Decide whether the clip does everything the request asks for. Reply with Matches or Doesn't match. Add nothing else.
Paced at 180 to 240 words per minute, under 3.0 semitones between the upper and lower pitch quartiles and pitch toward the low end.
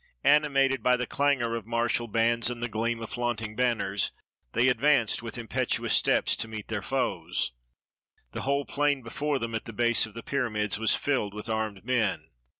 Matches